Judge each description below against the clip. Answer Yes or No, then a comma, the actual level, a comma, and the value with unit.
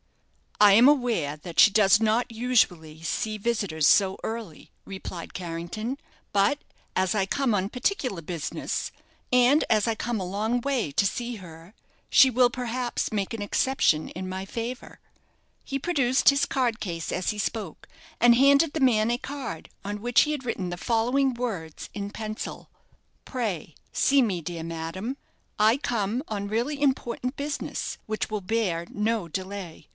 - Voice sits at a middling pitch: No, high, 220 Hz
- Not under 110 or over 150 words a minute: No, average, 160 wpm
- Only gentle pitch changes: No, average, 4.8 semitones